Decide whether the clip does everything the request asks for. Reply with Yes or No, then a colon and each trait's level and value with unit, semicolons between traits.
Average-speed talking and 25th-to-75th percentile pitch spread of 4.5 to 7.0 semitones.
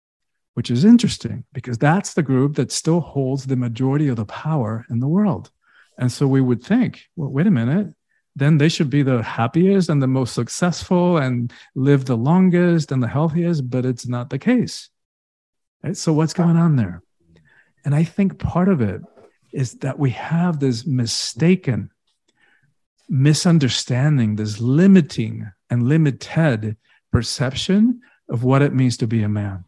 Yes: average, 165 wpm; wide, 5.6 semitones